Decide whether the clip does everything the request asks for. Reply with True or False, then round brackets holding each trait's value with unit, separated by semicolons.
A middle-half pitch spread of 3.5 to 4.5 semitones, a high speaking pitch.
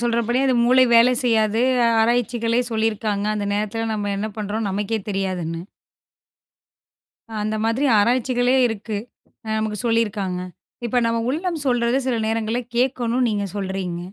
False (2.9 semitones; 225 Hz)